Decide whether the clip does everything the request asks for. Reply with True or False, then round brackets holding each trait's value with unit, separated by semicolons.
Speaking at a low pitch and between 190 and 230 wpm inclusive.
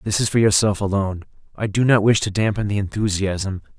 True (100 Hz; 205 wpm)